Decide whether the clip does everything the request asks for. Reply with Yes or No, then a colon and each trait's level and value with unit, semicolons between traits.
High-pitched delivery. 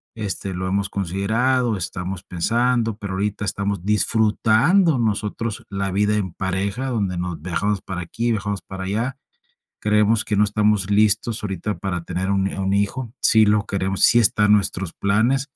No: low, 100 Hz